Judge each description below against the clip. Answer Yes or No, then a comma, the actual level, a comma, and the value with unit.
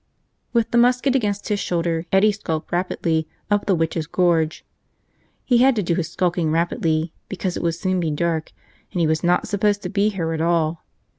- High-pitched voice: No, medium, 175 Hz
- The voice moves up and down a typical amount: Yes, average, 3.9 semitones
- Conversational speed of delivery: Yes, average, 195 wpm